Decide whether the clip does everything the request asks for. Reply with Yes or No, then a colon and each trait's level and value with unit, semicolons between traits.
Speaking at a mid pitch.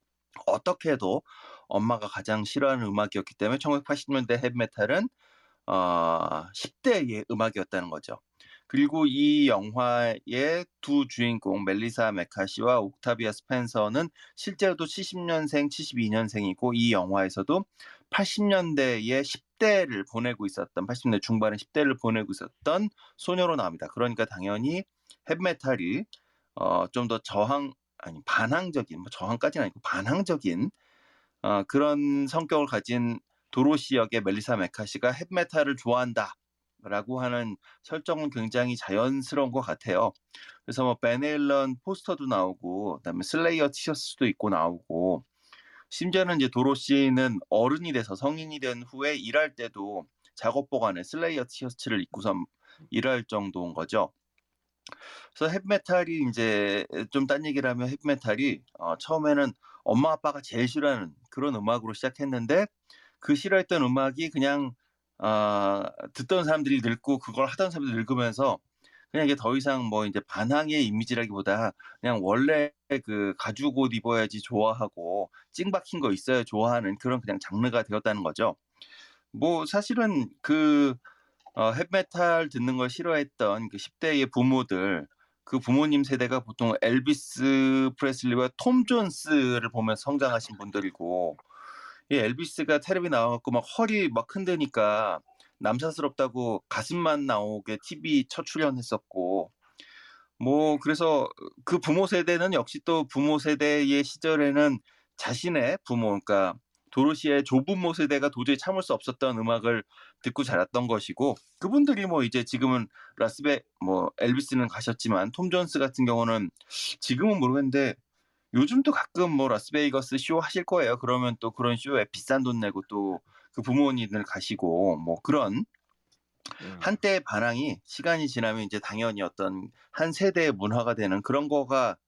No: low, 130 Hz